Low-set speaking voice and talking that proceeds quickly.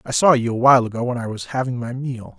Yes: low, 125 Hz; fast, 300 wpm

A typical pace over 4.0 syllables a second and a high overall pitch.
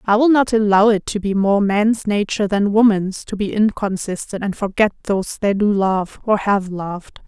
Yes: 4.9 syllables/s; high, 205 Hz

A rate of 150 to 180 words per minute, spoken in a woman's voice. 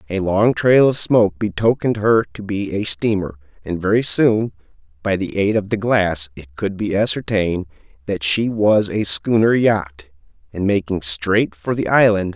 No: average, 175 wpm; male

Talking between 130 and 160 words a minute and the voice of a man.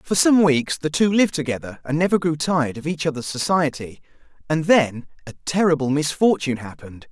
No: average, 175 wpm; male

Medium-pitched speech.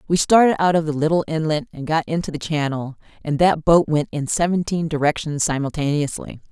Yes: medium, 155 Hz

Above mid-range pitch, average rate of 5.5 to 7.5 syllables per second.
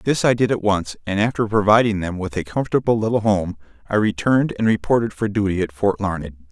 No: low, 105 Hz; 5.9 syllables/s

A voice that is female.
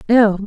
Yes: female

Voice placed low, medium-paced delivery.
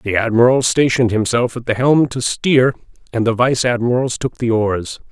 Yes: low, 120 Hz; average, 190 wpm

